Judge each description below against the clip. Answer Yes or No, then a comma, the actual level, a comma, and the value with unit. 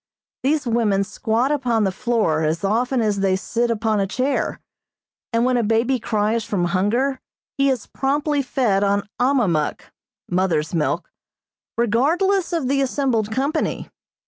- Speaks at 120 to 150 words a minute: Yes, average, 145 wpm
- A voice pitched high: Yes, high, 230 Hz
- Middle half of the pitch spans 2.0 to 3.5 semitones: No, average, 4.8 semitones